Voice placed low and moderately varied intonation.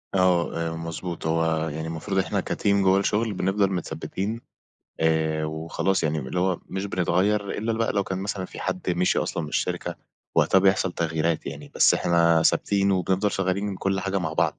Yes: very low, 90 Hz; average, 3.0 semitones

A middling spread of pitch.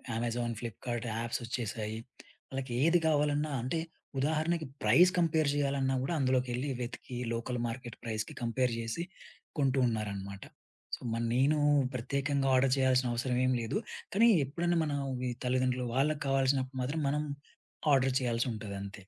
Yes: average, 3.2 semitones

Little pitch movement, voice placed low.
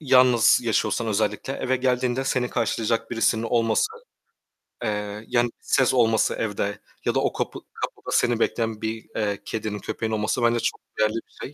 Yes: narrow, 2.3 semitones; low, 115 Hz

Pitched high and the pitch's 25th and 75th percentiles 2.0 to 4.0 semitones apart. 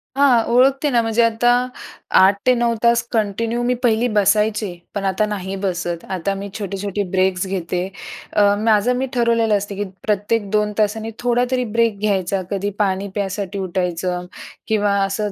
Yes: high, 205 Hz; average, 3.0 semitones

